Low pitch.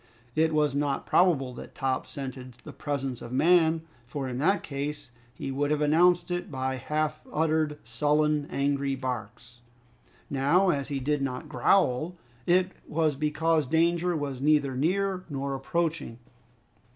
No: medium, 150 Hz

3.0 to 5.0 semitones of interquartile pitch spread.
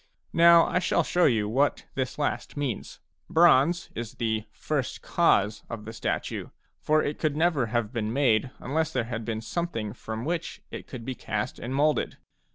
No: wide, 5.6 semitones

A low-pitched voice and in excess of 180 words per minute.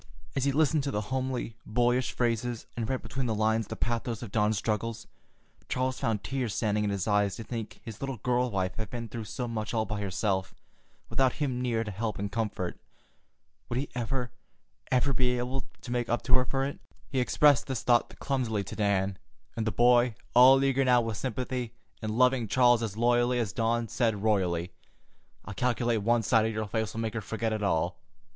Yes: low, 115 Hz; average, 200 wpm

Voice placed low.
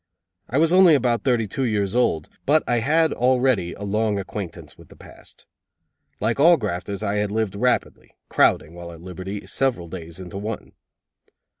Yes: low, 105 Hz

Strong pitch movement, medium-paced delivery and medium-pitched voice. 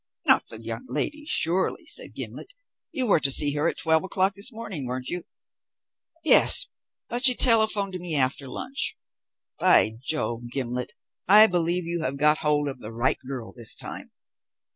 Yes: wide, 7.4 semitones; average, 170 wpm; medium, 160 Hz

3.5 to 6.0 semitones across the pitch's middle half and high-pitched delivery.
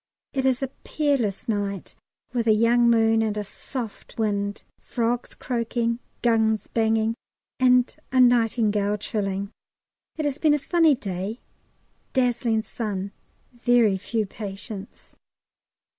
No: average, 2.9 semitones; high, 225 Hz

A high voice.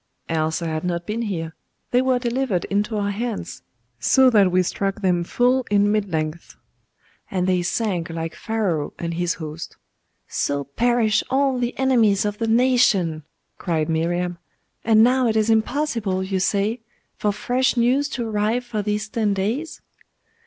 Yes: high, 210 Hz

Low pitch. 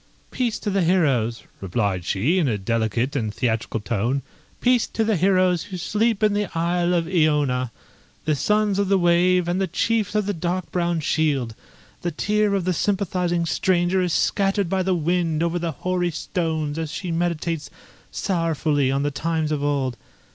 No: medium, 170 Hz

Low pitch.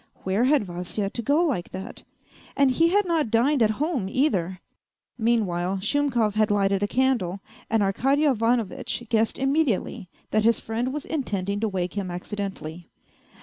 No: high, 220 Hz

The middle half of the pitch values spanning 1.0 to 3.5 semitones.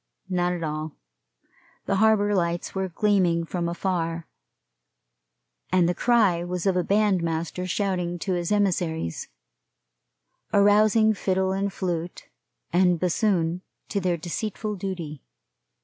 Yes: average, 2.7 semitones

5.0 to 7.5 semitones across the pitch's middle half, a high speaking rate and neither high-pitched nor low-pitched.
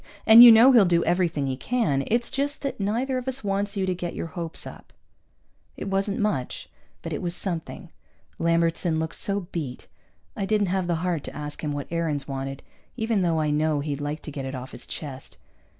Yes: wide, 5.4 semitones; fast, 210 wpm; medium, 170 Hz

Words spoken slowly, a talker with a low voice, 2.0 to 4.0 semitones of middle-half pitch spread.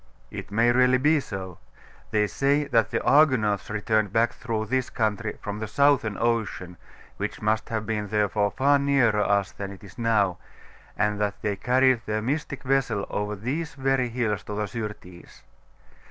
No: average, 170 wpm; low, 110 Hz; average, 3.7 semitones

